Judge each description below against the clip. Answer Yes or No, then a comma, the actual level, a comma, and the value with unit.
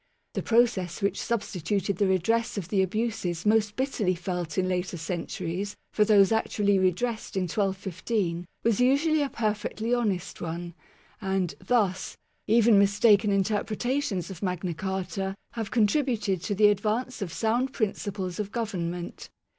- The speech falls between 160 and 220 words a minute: No, average, 145 wpm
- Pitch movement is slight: No, average, 3.3 semitones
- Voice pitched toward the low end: No, high, 200 Hz